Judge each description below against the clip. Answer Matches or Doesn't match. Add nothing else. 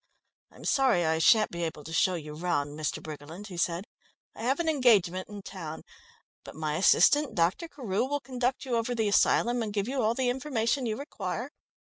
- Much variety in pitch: Matches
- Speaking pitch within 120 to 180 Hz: Doesn't match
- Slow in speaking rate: Doesn't match